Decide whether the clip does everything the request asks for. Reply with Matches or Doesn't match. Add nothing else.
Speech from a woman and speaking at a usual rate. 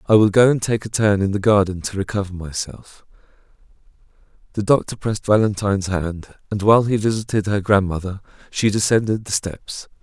Doesn't match